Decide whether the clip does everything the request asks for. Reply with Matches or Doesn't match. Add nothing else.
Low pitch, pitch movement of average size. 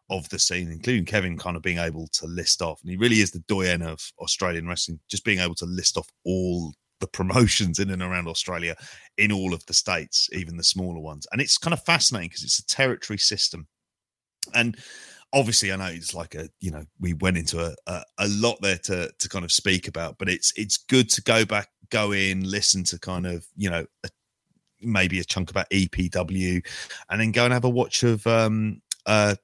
Matches